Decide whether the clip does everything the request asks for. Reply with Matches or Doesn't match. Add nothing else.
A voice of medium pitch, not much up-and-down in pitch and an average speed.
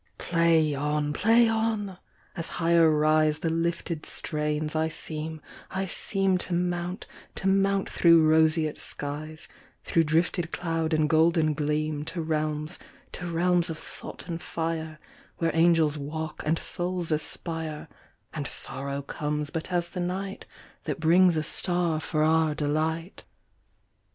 Doesn't match